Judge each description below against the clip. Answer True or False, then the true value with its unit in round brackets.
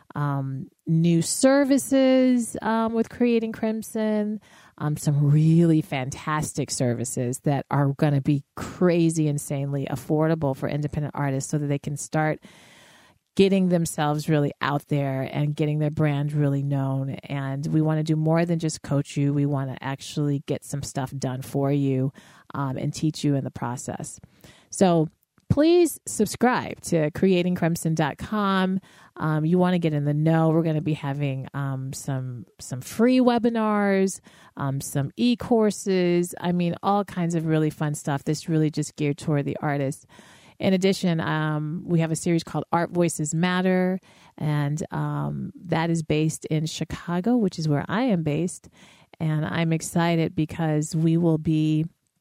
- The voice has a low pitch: False (155 Hz)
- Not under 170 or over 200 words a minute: False (155 wpm)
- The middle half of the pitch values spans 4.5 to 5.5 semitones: False (3.5 semitones)